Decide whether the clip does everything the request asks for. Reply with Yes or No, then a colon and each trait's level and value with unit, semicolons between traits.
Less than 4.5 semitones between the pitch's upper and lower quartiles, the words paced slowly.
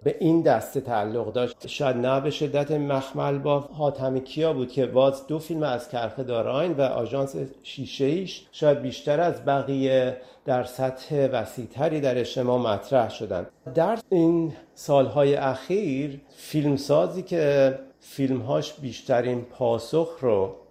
No: narrow, 2.6 semitones; average, 135 wpm